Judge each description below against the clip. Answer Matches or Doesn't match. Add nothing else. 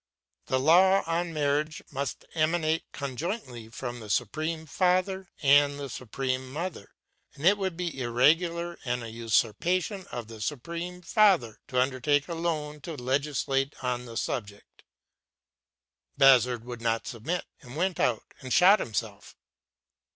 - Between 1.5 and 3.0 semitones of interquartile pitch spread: Doesn't match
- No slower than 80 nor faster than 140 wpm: Matches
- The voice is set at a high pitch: Doesn't match